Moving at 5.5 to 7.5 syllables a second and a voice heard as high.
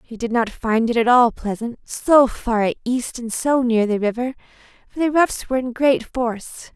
No: 4.7 syllables/s; high, 240 Hz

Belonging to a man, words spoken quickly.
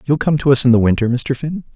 Yes: male; fast, 310 wpm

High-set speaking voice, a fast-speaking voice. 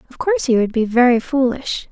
Yes: high, 245 Hz; fast, 220 wpm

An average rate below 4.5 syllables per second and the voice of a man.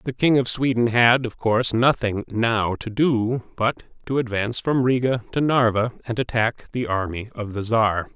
No: 4.7 syllables/s; male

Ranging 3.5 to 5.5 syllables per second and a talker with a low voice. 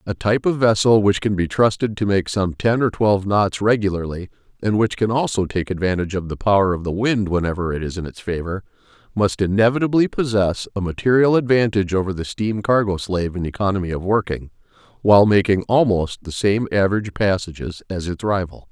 No: 5.9 syllables/s; low, 100 Hz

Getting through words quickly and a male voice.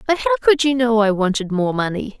No: fast, 245 wpm; female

